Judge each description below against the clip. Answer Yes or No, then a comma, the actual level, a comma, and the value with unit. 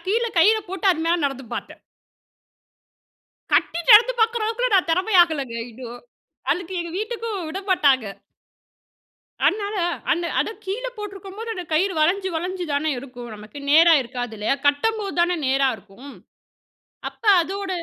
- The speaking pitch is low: No, very high, 355 Hz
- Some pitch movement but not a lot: No, wide, 6.4 semitones